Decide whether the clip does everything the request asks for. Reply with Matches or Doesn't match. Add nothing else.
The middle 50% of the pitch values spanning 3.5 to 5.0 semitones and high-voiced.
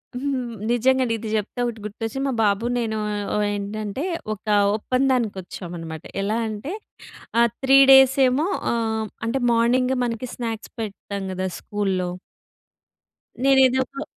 Matches